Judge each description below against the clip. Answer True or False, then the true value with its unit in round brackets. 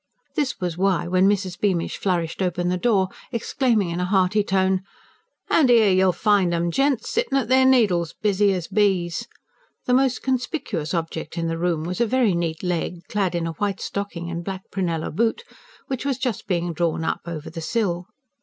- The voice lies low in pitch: False (190 Hz)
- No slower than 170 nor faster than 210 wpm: True (190 wpm)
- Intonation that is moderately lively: True (4.2 semitones)